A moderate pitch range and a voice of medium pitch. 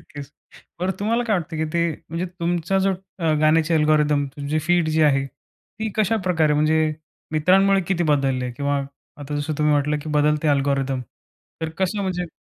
Yes: average, 3.4 semitones; medium, 155 Hz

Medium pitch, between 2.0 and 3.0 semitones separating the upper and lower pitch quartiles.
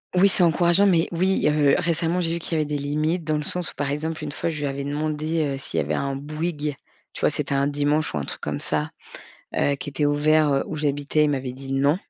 Yes: medium, 150 Hz; narrow, 2.4 semitones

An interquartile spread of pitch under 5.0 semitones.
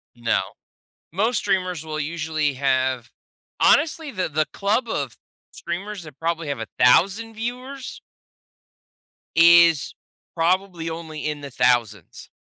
No: wide, 5.4 semitones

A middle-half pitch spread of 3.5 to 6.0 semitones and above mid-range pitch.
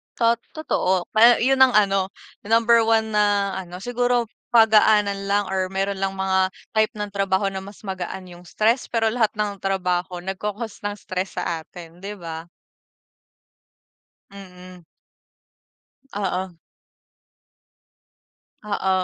No: narrow, 2.6 semitones; high, 200 Hz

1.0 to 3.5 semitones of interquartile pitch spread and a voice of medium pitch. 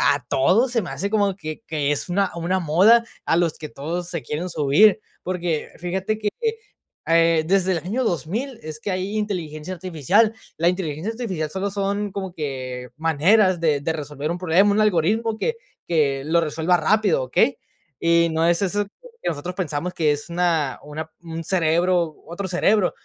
No: average, 4.1 semitones; medium, 175 Hz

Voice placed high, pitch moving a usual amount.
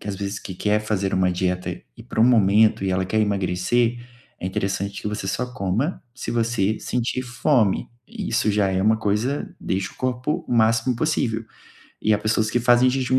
No: low, 110 Hz; average, 3.7 semitones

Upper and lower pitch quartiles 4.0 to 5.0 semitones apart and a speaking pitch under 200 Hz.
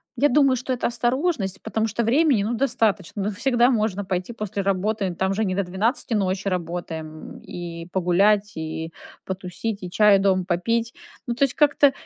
No: average, 4.3 semitones; high, 205 Hz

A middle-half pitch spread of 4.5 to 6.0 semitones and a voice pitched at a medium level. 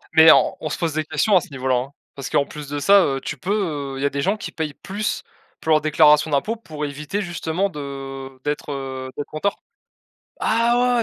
Yes: average, 5.3 semitones; medium, 150 Hz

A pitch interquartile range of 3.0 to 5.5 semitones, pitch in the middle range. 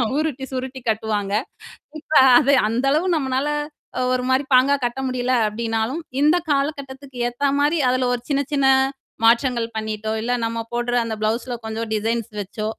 No: average, 3.5 semitones; very high, 250 Hz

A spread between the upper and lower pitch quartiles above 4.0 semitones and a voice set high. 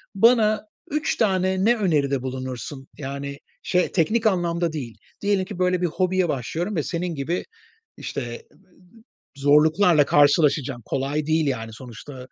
No: average, 5.1 semitones; medium, 160 Hz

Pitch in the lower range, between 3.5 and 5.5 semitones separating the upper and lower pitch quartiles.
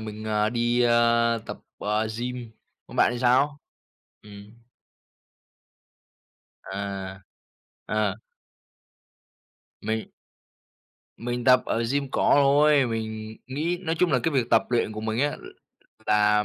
No: low, 115 Hz; average, 3.0 semitones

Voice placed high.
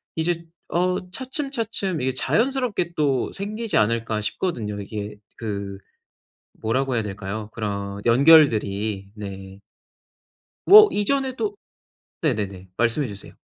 No: low, 120 Hz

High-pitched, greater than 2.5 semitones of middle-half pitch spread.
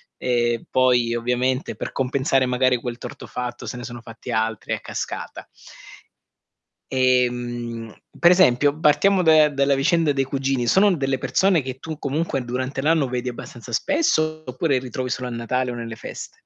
No: low, 130 Hz; average, 2.9 semitones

